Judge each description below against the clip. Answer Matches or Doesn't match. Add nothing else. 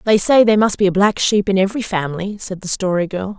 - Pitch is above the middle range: Matches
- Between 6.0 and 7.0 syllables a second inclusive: Matches